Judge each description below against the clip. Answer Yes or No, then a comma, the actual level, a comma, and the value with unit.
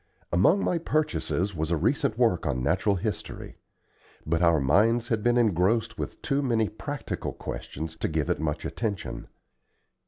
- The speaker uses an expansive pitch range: Yes, wide, 6.7 semitones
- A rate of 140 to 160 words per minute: Yes, average, 155 wpm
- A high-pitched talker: No, low, 100 Hz